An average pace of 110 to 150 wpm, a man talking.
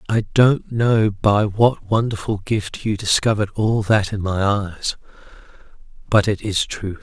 Yes: average, 145 wpm; male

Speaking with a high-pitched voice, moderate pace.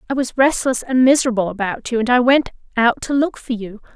No: high, 245 Hz; fast, 225 wpm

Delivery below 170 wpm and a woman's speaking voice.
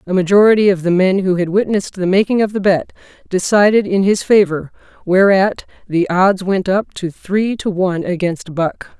No: average, 185 wpm; female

